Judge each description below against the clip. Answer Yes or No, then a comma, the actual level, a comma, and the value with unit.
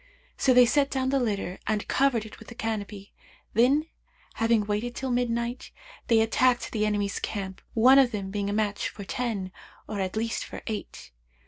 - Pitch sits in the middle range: No, high, 225 Hz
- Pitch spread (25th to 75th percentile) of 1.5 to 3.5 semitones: Yes, average, 3.1 semitones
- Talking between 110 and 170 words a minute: No, average, 185 wpm